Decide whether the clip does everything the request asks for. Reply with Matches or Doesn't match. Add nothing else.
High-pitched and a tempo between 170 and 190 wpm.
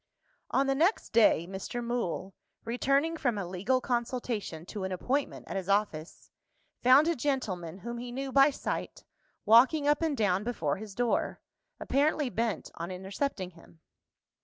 Doesn't match